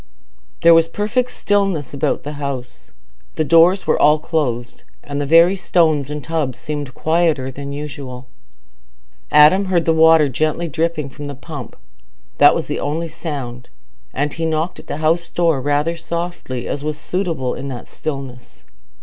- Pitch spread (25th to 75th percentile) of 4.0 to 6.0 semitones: No, average, 3.0 semitones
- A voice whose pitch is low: No, medium, 155 Hz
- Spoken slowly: No, average, 155 wpm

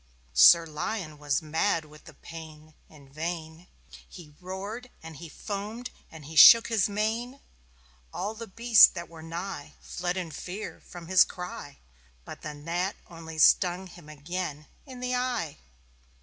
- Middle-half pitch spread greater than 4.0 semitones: Yes, average, 4.5 semitones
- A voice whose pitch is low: No, medium, 175 Hz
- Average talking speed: Yes, average, 150 wpm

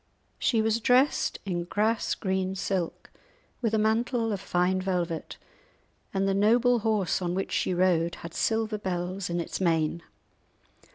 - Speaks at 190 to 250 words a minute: No, average, 150 wpm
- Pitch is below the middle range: No, high, 195 Hz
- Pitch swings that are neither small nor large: Yes, average, 3.8 semitones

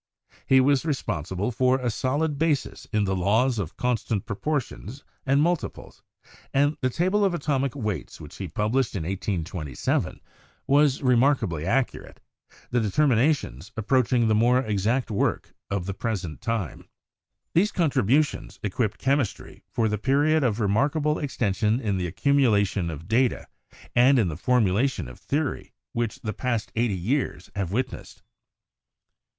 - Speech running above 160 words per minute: No, average, 145 wpm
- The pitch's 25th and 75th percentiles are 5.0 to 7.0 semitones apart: Yes, wide, 5.4 semitones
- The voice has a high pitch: No, low, 120 Hz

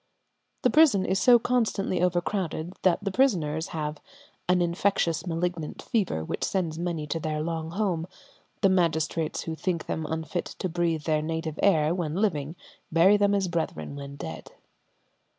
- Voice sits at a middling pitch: Yes, medium, 170 Hz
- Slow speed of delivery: No, average, 155 wpm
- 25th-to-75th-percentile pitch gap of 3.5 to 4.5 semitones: No, average, 3.1 semitones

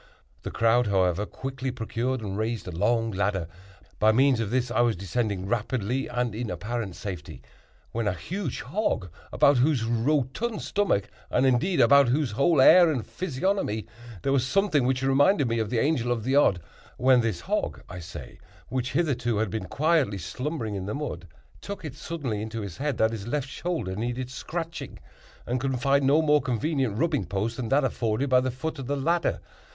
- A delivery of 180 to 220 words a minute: Yes, average, 185 wpm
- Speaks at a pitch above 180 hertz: No, low, 125 Hz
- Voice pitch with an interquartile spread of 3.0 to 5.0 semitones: Yes, average, 4.5 semitones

